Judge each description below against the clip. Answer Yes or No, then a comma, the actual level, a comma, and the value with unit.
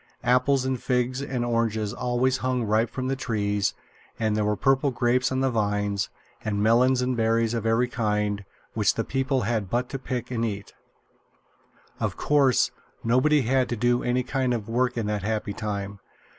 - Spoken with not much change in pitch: No, average, 3.2 semitones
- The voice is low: Yes, low, 120 Hz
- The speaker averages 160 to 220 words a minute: Yes, average, 180 wpm